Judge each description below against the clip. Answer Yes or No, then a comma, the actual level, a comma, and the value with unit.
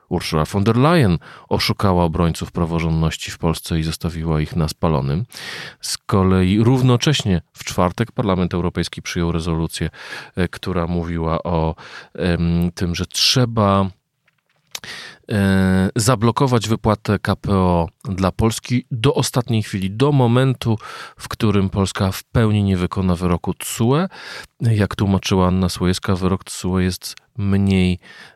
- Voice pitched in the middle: No, very low, 95 Hz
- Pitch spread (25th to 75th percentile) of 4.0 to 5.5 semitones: Yes, average, 4.4 semitones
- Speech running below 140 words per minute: Yes, average, 120 wpm